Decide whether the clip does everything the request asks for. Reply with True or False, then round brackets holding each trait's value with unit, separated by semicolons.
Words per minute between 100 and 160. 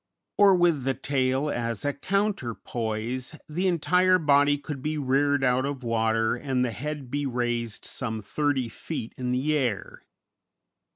True (150 wpm)